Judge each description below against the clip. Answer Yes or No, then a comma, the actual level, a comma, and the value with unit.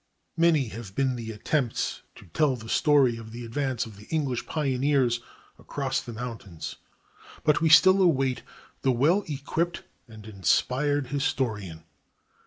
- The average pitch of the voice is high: No, low, 130 Hz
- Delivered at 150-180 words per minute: No, average, 140 wpm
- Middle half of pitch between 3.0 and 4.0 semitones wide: No, average, 4.5 semitones